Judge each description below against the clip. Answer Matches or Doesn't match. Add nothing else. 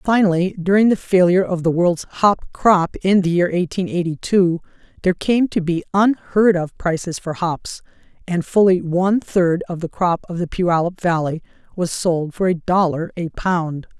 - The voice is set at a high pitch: Doesn't match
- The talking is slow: Doesn't match